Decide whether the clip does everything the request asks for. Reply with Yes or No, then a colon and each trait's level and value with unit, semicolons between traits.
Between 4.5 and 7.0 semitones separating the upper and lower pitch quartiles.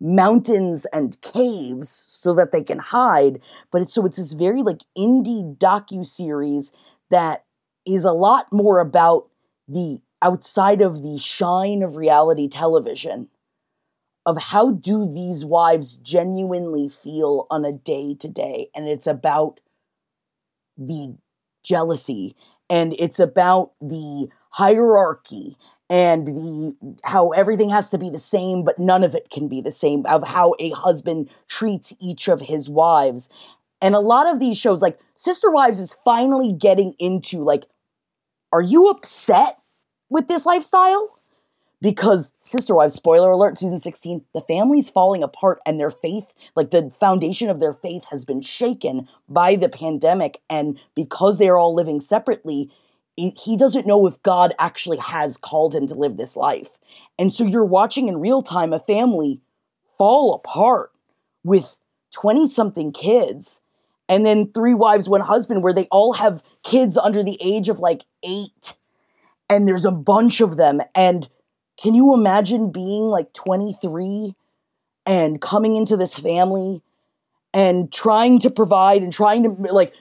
Yes: average, 4.8 semitones